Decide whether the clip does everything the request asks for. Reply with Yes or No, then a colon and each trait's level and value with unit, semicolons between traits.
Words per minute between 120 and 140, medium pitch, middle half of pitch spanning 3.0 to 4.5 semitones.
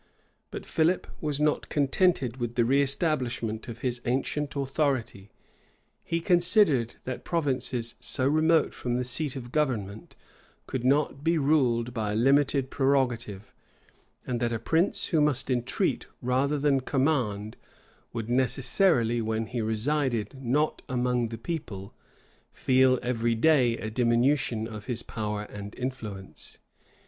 No: slow, 135 wpm; low, 125 Hz; average, 3.7 semitones